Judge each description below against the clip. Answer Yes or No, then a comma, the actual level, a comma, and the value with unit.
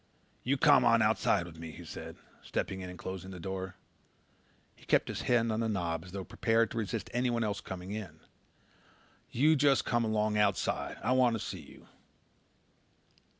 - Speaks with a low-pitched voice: Yes, low, 110 Hz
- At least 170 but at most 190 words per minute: Yes, average, 180 wpm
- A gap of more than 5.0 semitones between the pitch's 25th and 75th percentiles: No, average, 4.0 semitones